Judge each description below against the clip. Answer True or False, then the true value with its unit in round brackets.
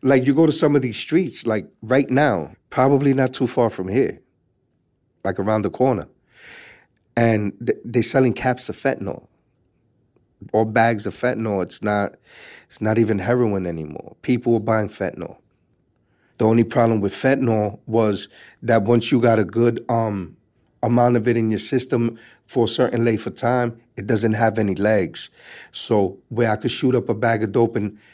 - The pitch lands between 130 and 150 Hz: False (115 Hz)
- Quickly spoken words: False (175 wpm)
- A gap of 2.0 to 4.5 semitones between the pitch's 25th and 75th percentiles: True (2.8 semitones)